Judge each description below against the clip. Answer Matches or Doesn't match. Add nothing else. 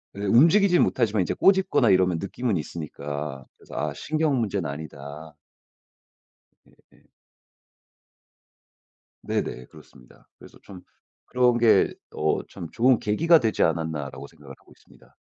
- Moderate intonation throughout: Doesn't match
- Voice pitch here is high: Doesn't match